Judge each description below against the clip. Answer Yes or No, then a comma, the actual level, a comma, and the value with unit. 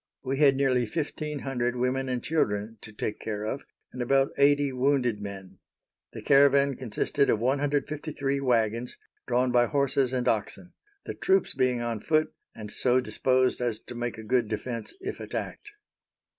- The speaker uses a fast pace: No, average, 160 wpm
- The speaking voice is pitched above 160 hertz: No, low, 125 Hz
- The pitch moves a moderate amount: Yes, average, 3.1 semitones